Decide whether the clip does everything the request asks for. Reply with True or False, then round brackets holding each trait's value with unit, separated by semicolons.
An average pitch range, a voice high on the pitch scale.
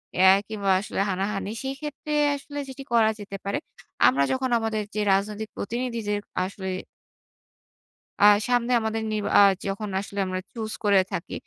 True (3.0 semitones; 215 Hz)